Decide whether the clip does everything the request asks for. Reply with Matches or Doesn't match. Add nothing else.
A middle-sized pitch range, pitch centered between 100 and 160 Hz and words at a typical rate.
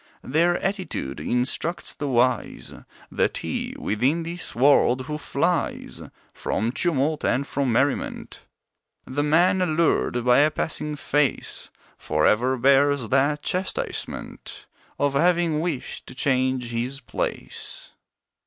Doesn't match